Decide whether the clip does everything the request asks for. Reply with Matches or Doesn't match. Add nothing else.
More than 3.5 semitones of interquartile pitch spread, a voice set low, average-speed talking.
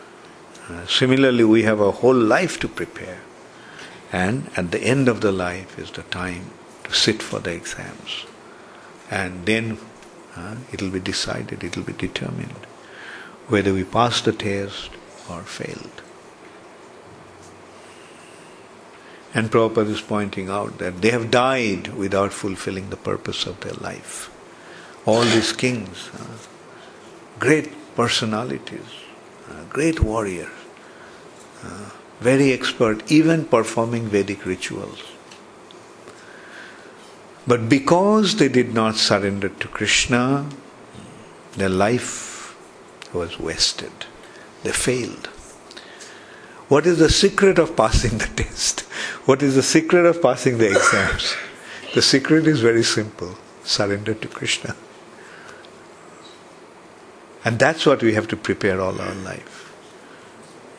Doesn't match